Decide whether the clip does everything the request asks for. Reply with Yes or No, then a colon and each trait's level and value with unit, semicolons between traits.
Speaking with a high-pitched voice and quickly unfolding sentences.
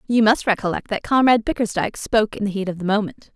Yes: high, 215 Hz; fast, 235 wpm